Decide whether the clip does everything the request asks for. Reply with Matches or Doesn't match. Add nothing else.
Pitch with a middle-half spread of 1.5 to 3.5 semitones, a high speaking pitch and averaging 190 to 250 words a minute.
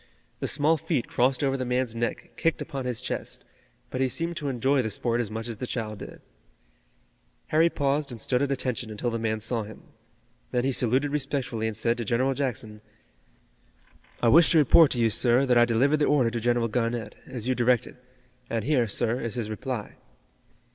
Doesn't match